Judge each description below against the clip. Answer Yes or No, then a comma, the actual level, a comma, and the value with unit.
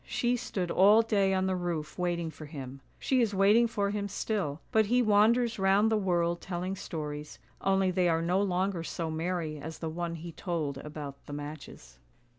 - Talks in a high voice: No, medium, 180 Hz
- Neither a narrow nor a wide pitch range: Yes, average, 4.1 semitones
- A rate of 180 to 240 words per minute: Yes, average, 190 wpm